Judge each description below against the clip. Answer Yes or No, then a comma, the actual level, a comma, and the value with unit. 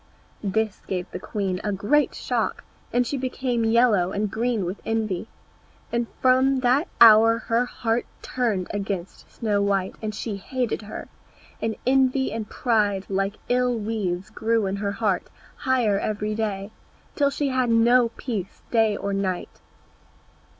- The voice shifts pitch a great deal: No, average, 3.5 semitones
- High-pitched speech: Yes, high, 220 Hz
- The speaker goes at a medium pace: Yes, average, 150 wpm